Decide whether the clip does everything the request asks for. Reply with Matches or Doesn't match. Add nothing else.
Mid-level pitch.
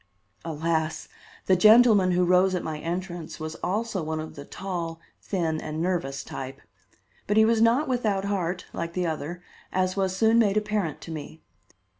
Matches